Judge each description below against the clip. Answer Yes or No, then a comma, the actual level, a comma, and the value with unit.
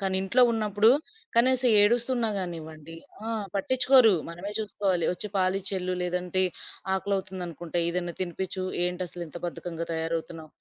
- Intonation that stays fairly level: No, average, 3.1 semitones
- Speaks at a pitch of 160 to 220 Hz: Yes, medium, 185 Hz